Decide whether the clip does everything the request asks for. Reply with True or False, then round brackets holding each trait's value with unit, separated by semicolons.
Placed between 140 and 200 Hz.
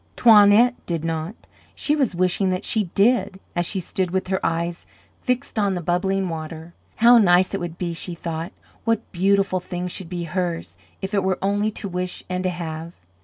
True (185 Hz)